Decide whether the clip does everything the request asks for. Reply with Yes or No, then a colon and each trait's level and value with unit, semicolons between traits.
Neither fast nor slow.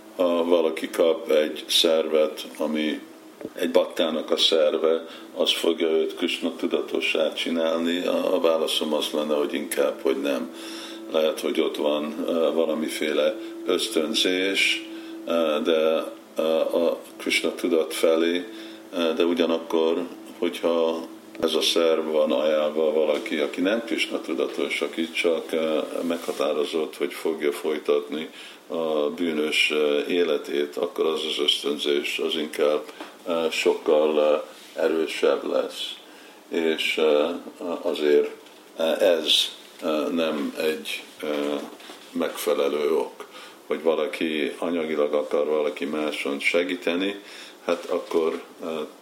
No: slow, 100 wpm